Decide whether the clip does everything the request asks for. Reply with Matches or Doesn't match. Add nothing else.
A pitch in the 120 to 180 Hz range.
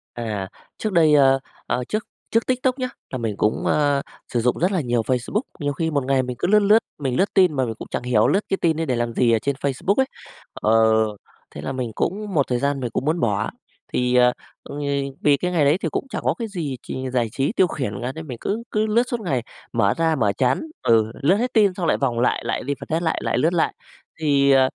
Matches